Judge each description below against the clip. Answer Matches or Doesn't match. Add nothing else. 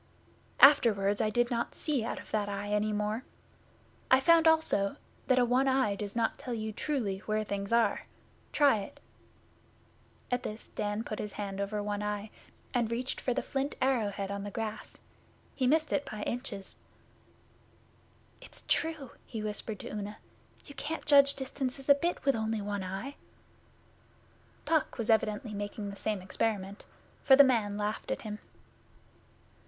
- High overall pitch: Matches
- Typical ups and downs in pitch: Matches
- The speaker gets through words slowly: Doesn't match